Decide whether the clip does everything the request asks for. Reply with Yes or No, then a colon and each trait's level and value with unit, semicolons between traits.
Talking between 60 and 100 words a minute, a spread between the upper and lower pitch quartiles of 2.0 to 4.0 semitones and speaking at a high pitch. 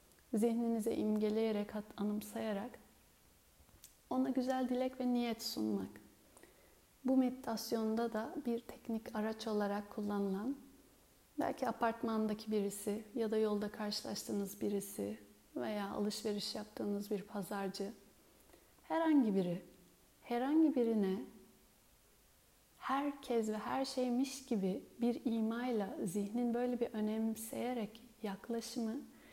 Yes: slow, 95 wpm; average, 2.9 semitones; high, 225 Hz